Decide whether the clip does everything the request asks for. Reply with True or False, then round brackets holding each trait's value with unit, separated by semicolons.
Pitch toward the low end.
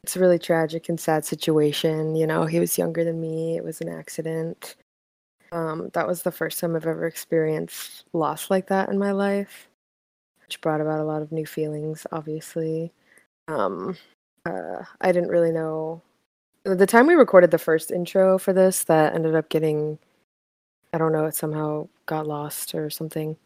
False (160 Hz)